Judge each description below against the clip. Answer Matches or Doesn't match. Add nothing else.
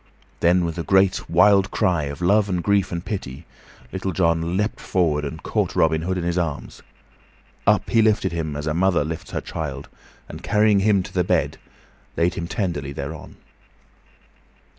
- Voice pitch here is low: Matches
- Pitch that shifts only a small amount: Doesn't match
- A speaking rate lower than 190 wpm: Matches